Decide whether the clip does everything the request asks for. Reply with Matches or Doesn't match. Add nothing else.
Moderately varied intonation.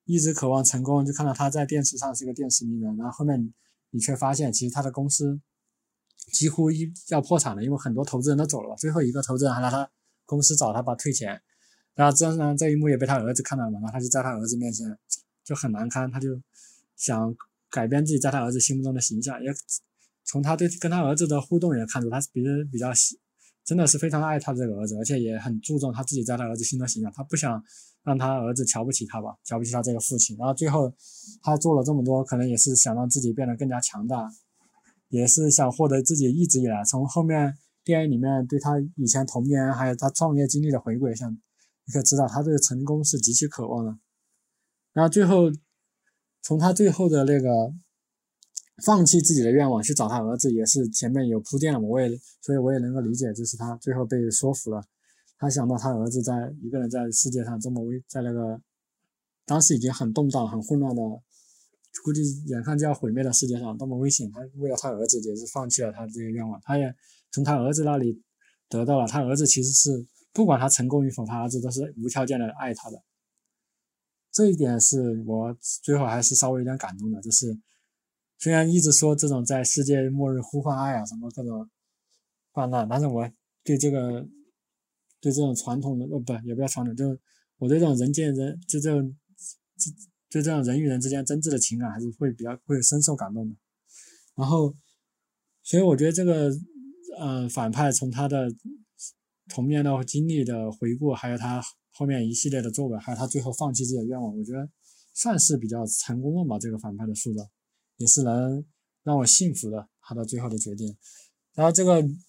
Matches